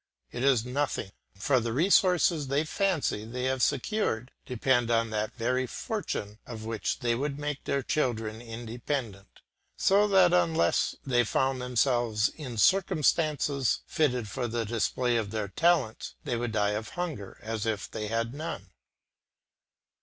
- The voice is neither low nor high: No, low, 125 Hz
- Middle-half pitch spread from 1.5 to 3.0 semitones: No, average, 4.6 semitones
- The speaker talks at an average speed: Yes, average, 145 wpm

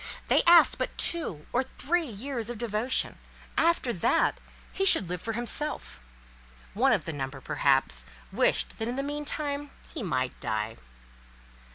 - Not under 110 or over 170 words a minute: Yes, average, 145 wpm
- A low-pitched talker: No, high, 240 Hz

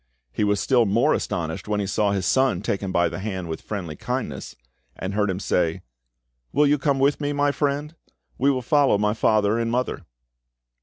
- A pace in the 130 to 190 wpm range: No, average, 200 wpm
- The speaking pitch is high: No, low, 105 Hz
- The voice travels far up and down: Yes, wide, 6.2 semitones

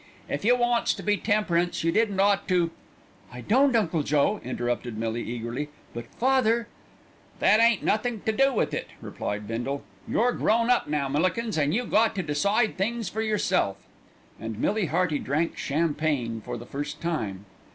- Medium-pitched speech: Yes, medium, 175 Hz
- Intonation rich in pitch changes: Yes, wide, 8.1 semitones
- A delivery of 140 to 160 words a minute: No, average, 175 wpm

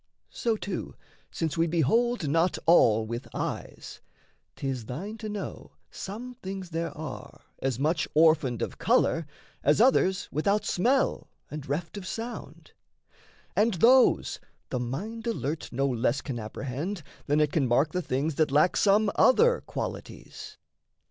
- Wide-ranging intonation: Yes, wide, 6.9 semitones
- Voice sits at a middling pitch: Yes, medium, 165 Hz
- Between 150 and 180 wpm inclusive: No, average, 140 wpm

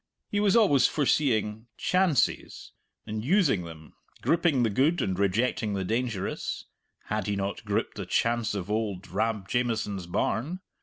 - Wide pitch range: Yes, wide, 5.8 semitones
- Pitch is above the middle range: No, low, 110 Hz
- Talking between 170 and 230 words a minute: No, average, 145 wpm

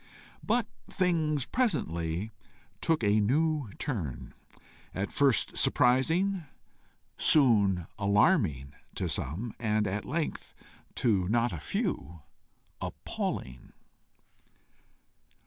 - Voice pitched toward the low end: Yes, low, 110 Hz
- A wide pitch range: Yes, wide, 8.7 semitones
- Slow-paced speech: Yes, slow, 85 wpm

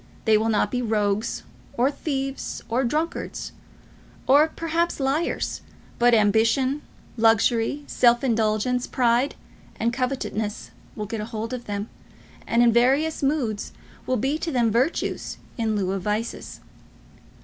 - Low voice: No, high, 240 Hz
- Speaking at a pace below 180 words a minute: Yes, slow, 135 wpm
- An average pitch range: Yes, average, 3.6 semitones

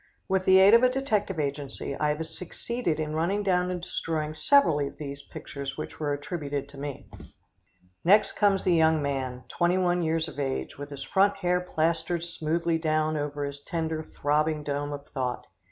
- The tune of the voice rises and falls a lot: No, average, 3.7 semitones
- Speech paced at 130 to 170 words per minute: No, average, 180 wpm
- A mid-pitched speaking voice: Yes, medium, 160 Hz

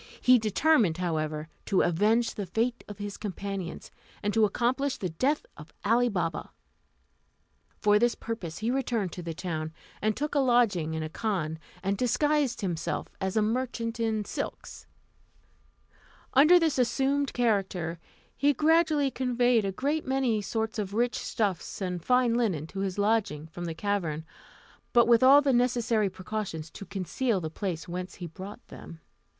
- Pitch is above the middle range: Yes, high, 215 Hz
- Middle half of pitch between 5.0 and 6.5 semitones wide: Yes, average, 5.3 semitones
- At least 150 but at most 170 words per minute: Yes, average, 160 wpm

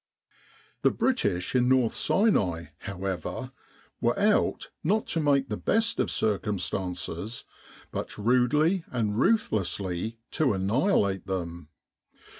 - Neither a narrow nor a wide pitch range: No, wide, 7.1 semitones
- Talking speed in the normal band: No, slow, 105 wpm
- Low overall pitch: Yes, low, 110 Hz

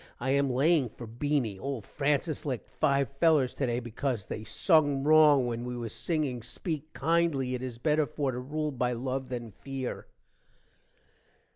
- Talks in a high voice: No, low, 135 Hz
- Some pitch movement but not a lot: Yes, average, 3.4 semitones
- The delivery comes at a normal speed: Yes, average, 160 wpm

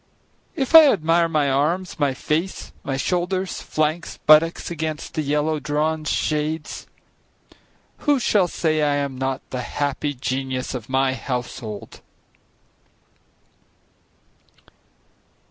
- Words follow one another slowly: Yes, slow, 110 wpm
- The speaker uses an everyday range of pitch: Yes, average, 3.6 semitones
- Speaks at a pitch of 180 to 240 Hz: No, medium, 150 Hz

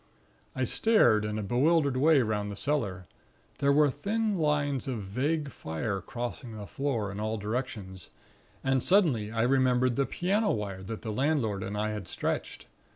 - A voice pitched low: Yes, low, 120 Hz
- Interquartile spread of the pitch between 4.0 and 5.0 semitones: No, wide, 5.4 semitones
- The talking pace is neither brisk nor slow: Yes, average, 165 wpm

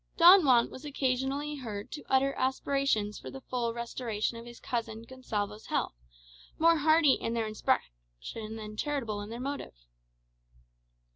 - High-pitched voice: Yes, high, 240 Hz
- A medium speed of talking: Yes, average, 145 wpm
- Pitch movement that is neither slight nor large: Yes, average, 4.2 semitones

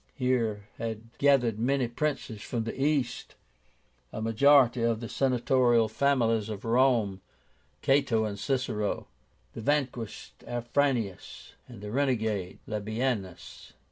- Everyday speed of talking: No, slow, 110 wpm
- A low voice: Yes, low, 120 Hz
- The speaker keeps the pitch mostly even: No, average, 3.5 semitones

